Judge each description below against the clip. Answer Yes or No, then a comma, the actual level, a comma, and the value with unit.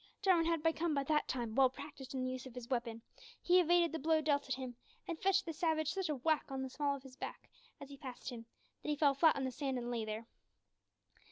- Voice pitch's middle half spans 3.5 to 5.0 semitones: Yes, average, 3.8 semitones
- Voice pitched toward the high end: Yes, very high, 280 Hz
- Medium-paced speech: No, fast, 255 wpm